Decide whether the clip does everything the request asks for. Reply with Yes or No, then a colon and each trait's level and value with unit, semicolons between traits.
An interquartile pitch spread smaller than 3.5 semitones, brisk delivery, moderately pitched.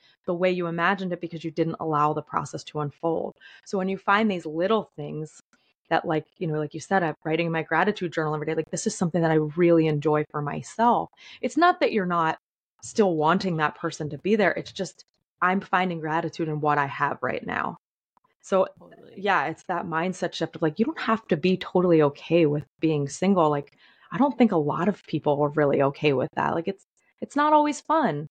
No: average, 3.8 semitones; fast, 225 wpm; medium, 165 Hz